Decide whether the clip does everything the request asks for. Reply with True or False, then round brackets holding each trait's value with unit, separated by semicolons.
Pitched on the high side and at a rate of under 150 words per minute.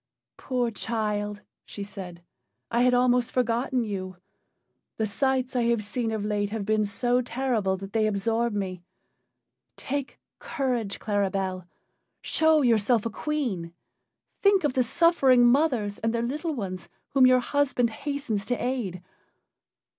True (235 Hz; 140 wpm)